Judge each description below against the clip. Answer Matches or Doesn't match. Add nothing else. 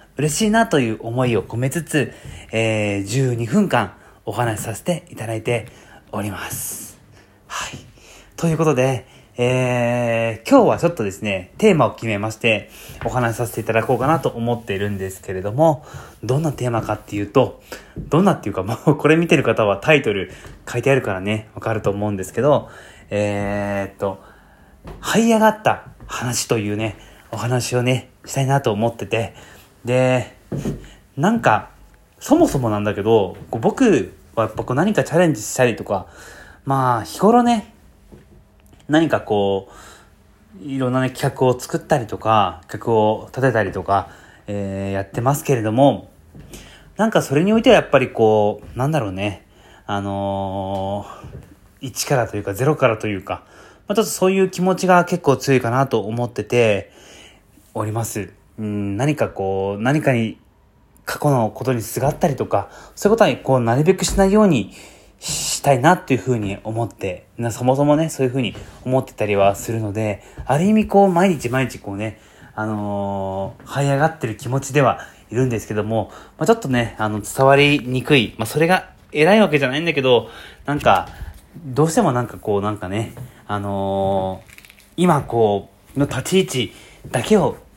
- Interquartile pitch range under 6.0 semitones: Matches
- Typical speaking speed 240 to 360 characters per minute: Matches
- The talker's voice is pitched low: Matches